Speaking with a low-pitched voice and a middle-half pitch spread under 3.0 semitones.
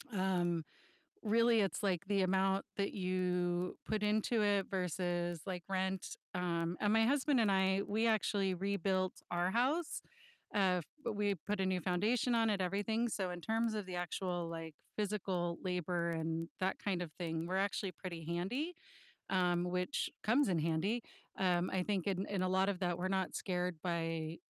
No: medium, 185 Hz; narrow, 2.6 semitones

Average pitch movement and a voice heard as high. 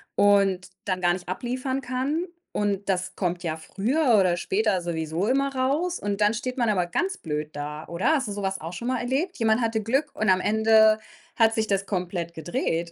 No: wide, 5.8 semitones; high, 205 Hz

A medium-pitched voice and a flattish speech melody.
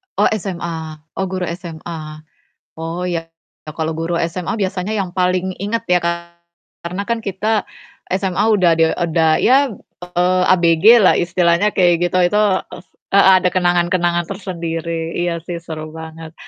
Yes: medium, 175 Hz; narrow, 2.1 semitones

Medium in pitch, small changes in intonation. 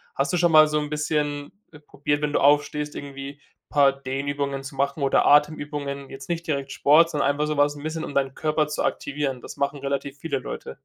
Yes: medium, 145 Hz; narrow, 1.3 semitones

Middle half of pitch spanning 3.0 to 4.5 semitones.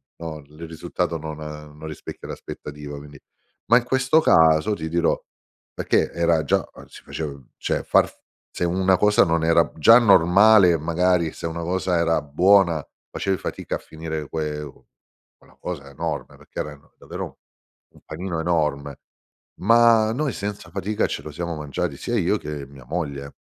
Yes: average, 3.7 semitones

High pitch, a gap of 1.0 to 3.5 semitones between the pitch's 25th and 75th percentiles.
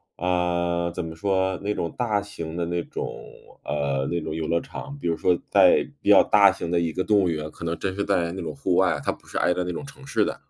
No: very low, 85 Hz; narrow, 2.4 semitones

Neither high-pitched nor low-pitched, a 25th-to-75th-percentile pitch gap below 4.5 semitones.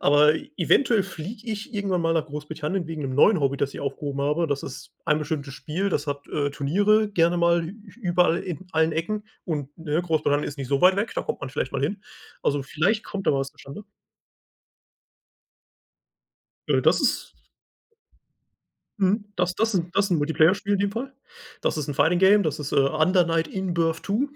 No: medium, 165 Hz; average, 5.1 semitones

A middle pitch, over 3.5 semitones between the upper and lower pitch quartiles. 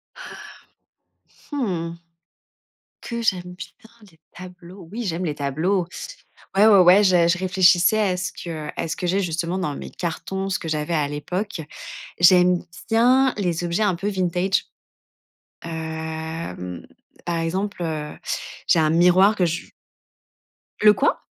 No: medium, 180 Hz; average, 2.8 semitones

